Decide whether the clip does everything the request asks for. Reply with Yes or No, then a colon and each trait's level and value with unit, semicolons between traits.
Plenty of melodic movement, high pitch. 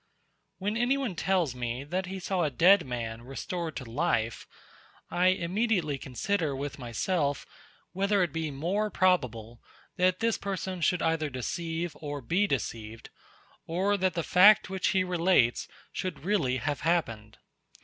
No: wide, 5.8 semitones; medium, 170 Hz